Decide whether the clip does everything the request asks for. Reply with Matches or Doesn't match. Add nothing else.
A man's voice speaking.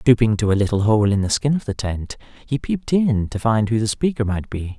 Matches